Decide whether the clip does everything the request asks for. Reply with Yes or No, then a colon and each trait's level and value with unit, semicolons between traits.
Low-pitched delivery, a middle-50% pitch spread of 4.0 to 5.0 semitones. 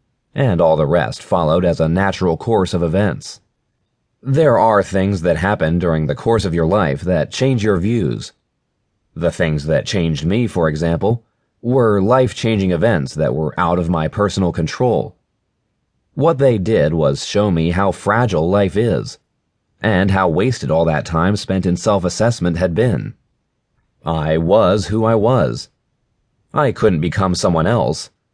Yes: very low, 95 Hz; average, 4.3 semitones